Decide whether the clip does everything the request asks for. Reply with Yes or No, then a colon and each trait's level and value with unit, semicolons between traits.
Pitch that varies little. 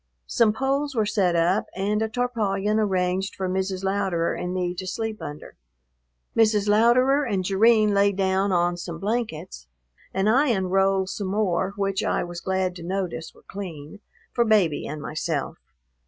No: average, 3.0 semitones